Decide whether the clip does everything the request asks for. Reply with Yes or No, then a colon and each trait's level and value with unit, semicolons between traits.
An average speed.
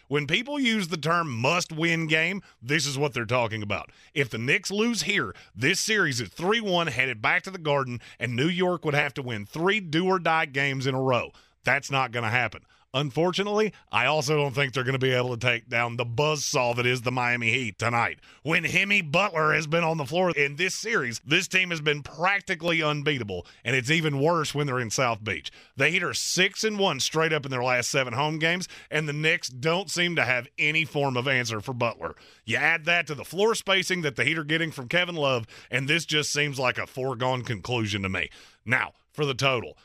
No: fast, 230 wpm